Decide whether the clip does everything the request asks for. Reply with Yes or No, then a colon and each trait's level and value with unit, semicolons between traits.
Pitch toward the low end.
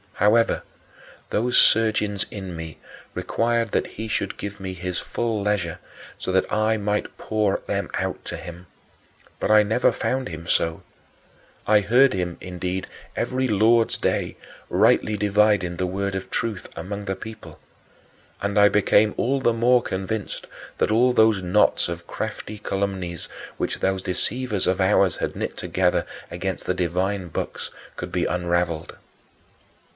Yes: low, 100 Hz